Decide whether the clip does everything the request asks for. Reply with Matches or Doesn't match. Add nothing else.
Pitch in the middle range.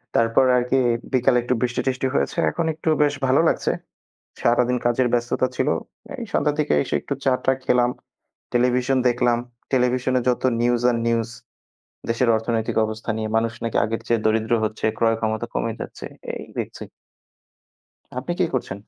Doesn't match